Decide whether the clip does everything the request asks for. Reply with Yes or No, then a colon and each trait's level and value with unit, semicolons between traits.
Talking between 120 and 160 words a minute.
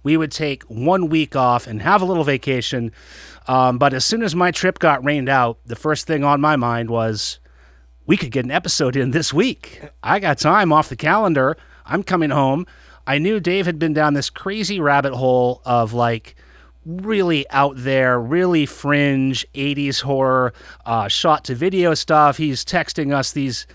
No: average, 185 wpm